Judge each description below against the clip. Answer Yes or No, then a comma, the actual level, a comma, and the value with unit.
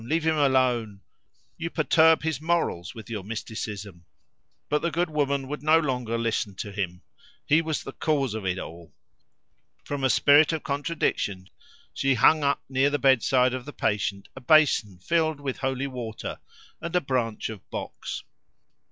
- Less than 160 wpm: No, average, 165 wpm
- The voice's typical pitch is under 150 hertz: Yes, low, 135 Hz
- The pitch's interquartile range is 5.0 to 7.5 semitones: Yes, wide, 5.6 semitones